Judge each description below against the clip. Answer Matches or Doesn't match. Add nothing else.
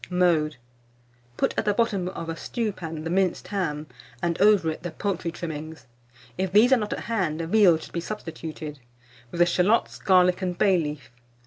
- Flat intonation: Doesn't match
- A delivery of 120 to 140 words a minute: Doesn't match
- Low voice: Doesn't match